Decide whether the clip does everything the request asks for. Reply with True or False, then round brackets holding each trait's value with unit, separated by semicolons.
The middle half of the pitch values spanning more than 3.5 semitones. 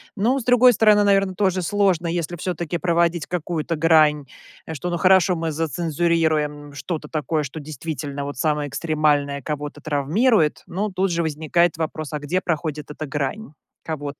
False (3.2 semitones)